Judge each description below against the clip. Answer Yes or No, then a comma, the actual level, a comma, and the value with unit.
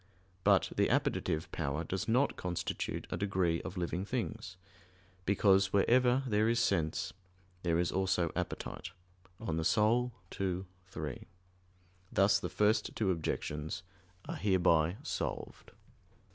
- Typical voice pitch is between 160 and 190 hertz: No, very low, 95 Hz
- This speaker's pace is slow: Yes, slow, 120 wpm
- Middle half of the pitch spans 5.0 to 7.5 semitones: No, average, 3.9 semitones